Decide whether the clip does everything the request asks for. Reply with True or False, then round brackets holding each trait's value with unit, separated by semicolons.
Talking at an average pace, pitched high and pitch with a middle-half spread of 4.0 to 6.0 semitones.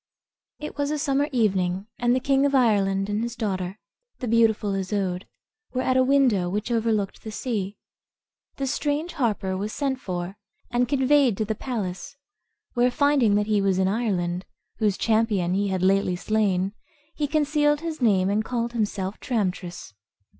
True (165 wpm; 220 Hz; 4.9 semitones)